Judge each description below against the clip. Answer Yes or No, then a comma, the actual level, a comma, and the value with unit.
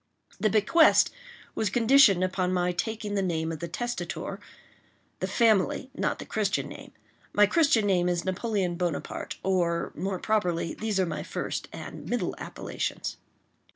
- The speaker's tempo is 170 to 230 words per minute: No, average, 140 wpm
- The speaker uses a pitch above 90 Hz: Yes, high, 190 Hz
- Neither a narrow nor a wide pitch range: Yes, average, 3.7 semitones